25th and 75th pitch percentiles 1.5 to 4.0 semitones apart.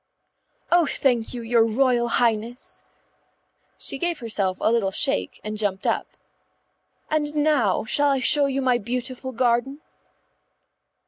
Yes: average, 3.5 semitones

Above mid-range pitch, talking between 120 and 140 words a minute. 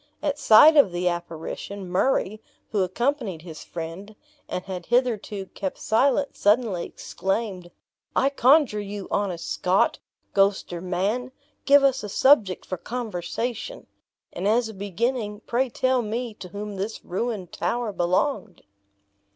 Yes: high, 210 Hz; slow, 135 wpm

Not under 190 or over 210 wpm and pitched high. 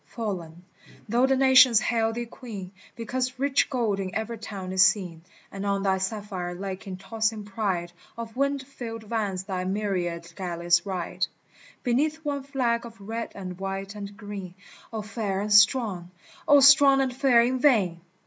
No: average, 165 wpm; high, 210 Hz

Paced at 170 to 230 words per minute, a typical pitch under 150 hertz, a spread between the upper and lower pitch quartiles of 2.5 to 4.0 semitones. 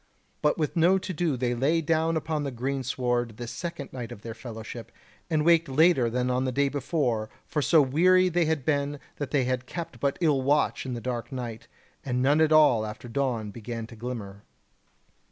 No: average, 200 wpm; low, 135 Hz; average, 4.4 semitones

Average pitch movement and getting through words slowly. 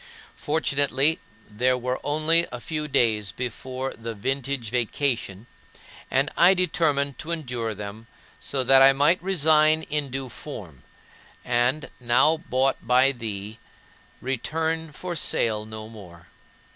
Yes: average, 4.8 semitones; slow, 125 wpm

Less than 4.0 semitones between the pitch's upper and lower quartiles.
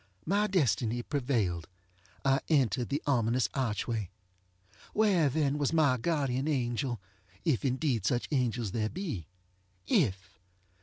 No: average, 4.6 semitones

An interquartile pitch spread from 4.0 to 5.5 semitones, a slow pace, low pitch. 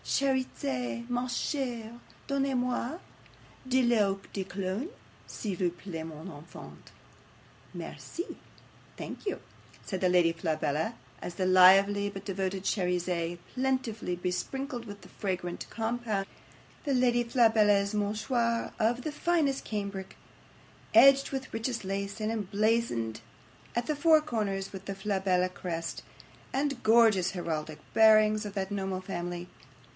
No: average, 4.6 semitones; slow, 125 wpm; high, 205 Hz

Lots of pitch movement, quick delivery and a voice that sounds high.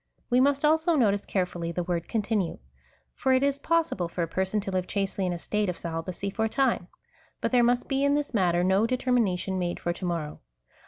Yes: wide, 6.2 semitones; fast, 220 wpm; high, 200 Hz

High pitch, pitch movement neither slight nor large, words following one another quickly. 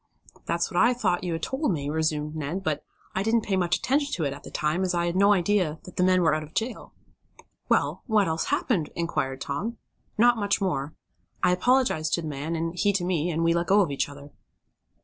No: medium, 175 Hz; average, 4.5 semitones; fast, 230 wpm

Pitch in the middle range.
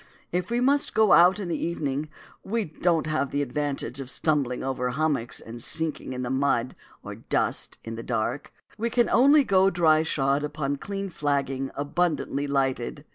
Yes: medium, 145 Hz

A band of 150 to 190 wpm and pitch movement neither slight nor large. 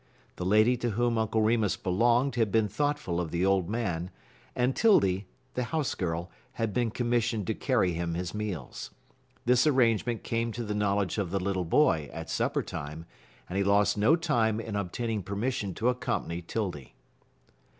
Yes: average, 170 wpm; average, 4.5 semitones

